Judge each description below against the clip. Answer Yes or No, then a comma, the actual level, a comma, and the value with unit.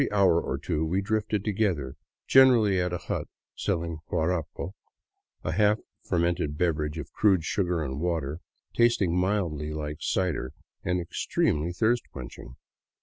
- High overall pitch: No, very low, 85 Hz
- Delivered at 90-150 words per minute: Yes, average, 145 wpm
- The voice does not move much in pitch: No, average, 4.3 semitones